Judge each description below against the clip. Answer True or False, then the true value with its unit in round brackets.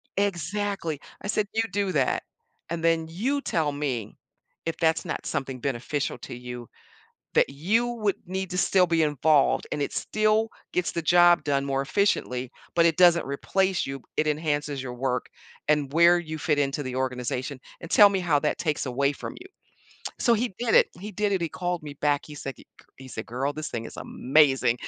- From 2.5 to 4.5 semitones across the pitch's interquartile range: False (5.1 semitones)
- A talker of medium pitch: True (155 Hz)